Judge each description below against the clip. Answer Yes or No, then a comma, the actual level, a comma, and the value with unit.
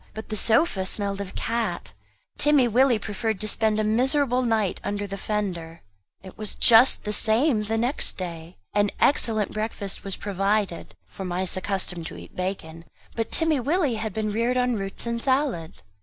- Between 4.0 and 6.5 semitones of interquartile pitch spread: No, average, 3.3 semitones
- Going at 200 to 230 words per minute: No, average, 170 wpm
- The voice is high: Yes, high, 215 Hz